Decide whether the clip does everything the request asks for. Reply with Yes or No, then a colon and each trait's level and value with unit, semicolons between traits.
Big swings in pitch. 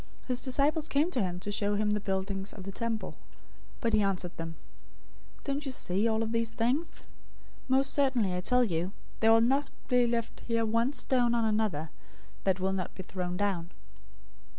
No: average, 4.5 semitones